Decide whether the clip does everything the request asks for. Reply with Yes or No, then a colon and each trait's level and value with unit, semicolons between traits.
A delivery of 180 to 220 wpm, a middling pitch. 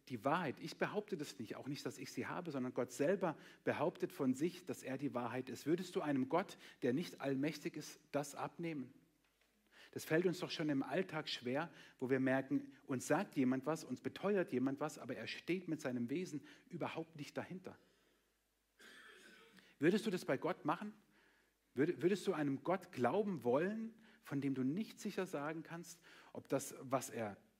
Yes: average, 185 wpm; medium, 155 Hz